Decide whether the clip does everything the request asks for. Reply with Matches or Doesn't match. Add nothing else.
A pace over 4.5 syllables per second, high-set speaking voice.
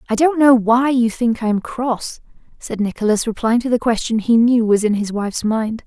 Matches